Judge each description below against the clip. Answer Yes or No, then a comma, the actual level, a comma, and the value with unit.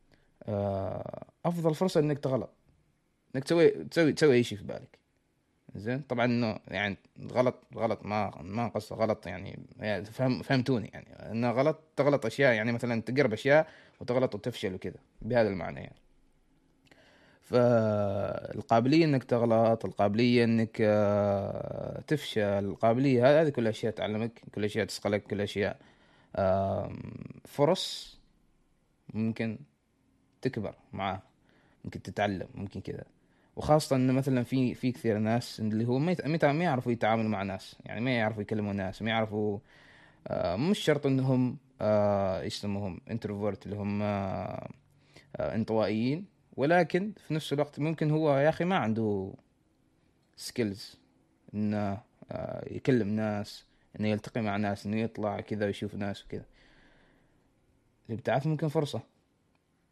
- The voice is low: Yes, low, 115 Hz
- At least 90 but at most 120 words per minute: No, average, 130 wpm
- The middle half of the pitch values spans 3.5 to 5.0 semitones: Yes, average, 4.2 semitones